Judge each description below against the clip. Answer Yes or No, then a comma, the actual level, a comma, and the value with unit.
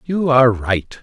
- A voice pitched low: Yes, low, 125 Hz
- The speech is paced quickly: No, average, 175 wpm